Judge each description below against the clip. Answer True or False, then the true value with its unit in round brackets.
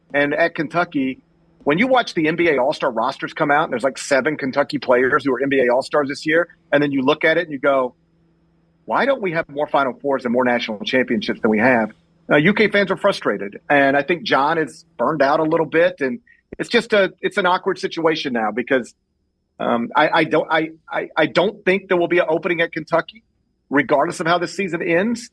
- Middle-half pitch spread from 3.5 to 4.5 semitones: True (3.8 semitones)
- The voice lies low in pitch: False (165 Hz)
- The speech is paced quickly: True (225 wpm)